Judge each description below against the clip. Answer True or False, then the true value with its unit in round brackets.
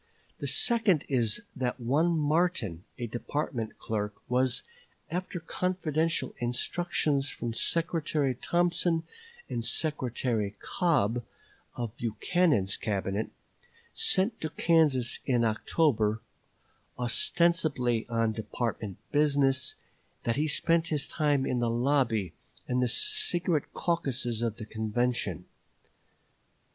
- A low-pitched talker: True (130 Hz)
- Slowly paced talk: True (105 wpm)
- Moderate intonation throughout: False (5.9 semitones)